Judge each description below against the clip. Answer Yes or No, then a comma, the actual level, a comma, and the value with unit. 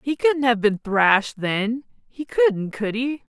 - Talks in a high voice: Yes, high, 240 Hz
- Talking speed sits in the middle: Yes, average, 180 wpm